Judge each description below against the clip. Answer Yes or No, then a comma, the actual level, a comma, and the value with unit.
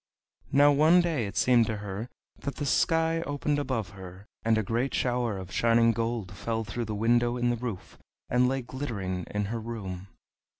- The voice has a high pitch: No, low, 115 Hz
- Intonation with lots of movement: No, average, 3.7 semitones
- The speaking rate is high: No, average, 185 wpm